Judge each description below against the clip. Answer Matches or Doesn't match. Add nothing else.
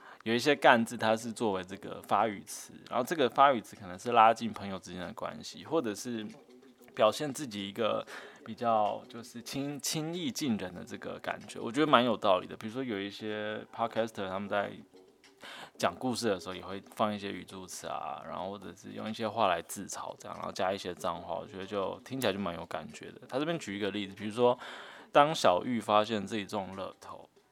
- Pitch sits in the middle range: Doesn't match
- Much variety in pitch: Doesn't match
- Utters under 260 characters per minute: Doesn't match